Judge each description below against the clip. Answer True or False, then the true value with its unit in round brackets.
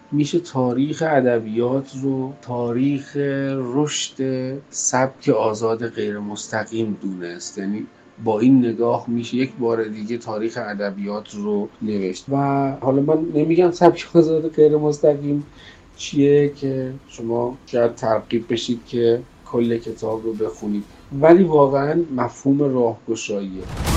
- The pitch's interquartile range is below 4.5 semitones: True (4.1 semitones)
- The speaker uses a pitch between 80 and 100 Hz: False (120 Hz)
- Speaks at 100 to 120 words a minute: True (115 wpm)